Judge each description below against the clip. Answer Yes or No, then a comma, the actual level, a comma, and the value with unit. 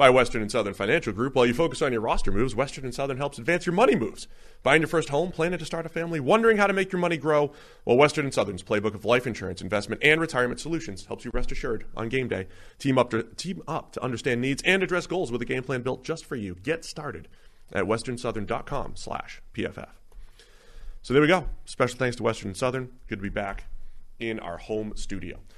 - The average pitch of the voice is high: No, low, 125 Hz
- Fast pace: Yes, fast, 230 wpm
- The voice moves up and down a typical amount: No, wide, 6.7 semitones